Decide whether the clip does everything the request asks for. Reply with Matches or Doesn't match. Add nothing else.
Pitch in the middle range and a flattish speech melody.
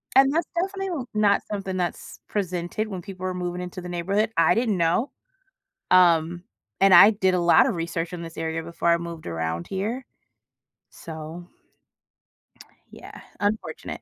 Doesn't match